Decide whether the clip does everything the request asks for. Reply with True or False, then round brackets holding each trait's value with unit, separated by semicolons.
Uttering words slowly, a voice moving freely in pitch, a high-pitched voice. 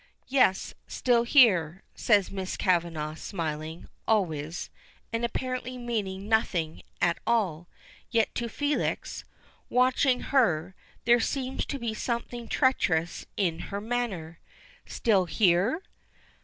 True (110 wpm; 5.9 semitones; 210 Hz)